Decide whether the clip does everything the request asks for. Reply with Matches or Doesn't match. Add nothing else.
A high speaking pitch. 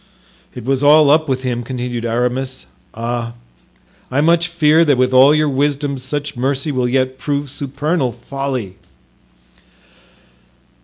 Doesn't match